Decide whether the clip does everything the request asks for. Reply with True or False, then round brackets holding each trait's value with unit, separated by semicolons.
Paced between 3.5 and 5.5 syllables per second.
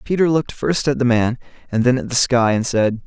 False (5.7 syllables/s)